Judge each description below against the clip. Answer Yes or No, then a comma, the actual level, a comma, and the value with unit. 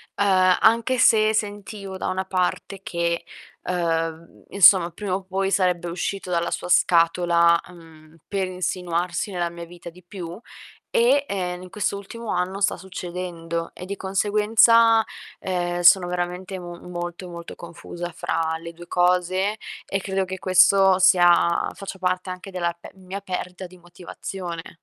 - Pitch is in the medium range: Yes, medium, 180 Hz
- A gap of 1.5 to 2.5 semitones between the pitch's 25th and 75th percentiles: Yes, narrow, 1.9 semitones